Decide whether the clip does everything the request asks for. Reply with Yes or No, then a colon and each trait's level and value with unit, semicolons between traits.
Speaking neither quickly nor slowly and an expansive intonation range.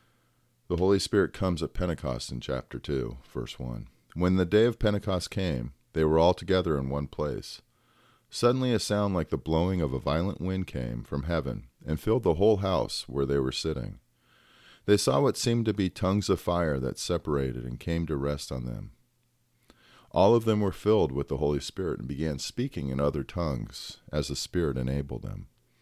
Yes: average, 195 wpm; wide, 6.1 semitones